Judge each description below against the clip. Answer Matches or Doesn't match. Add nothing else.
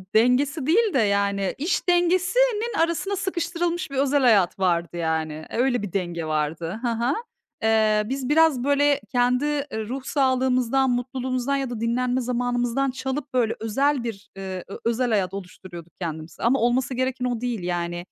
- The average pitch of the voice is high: Matches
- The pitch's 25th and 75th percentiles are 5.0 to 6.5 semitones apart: Matches